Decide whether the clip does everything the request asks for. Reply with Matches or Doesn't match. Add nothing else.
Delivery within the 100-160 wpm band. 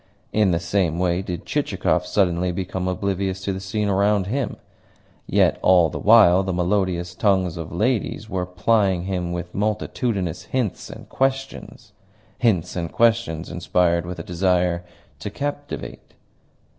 Matches